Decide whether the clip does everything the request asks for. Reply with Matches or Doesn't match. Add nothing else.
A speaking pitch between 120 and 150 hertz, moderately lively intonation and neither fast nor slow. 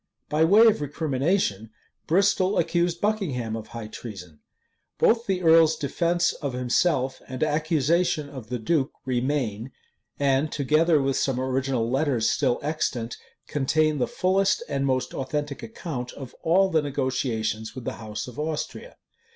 Matches